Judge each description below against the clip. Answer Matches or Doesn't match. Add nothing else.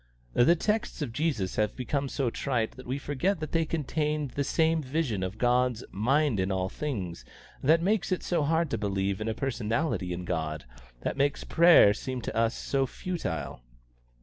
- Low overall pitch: Matches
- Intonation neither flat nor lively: Doesn't match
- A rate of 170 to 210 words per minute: Matches